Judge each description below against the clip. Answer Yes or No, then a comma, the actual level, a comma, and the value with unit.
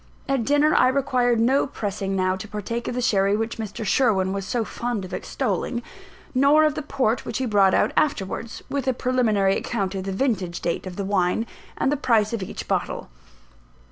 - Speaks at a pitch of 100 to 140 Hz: No, high, 225 Hz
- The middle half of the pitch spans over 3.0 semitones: Yes, average, 4.6 semitones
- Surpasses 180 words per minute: Yes, average, 200 wpm